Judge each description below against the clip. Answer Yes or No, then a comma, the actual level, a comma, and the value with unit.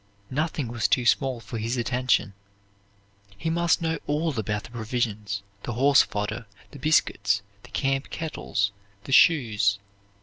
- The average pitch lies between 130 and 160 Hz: No, low, 120 Hz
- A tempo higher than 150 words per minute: No, average, 140 wpm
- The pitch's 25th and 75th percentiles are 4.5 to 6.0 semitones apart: Yes, average, 5.2 semitones